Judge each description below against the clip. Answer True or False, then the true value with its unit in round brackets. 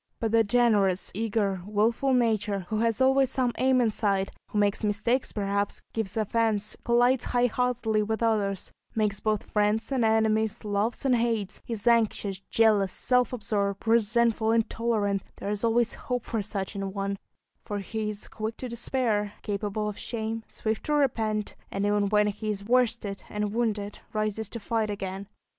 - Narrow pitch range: True (2.2 semitones)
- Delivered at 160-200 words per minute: True (165 wpm)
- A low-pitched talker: False (215 Hz)